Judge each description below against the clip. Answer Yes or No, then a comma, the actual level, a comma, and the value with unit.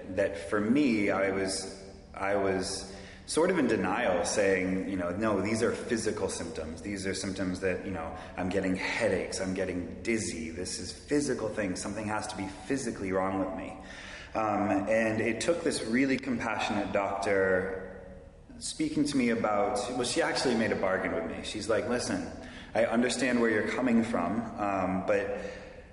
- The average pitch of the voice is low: Yes, very low, 95 Hz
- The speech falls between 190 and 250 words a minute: No, average, 170 wpm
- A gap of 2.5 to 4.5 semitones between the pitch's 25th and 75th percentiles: Yes, average, 2.9 semitones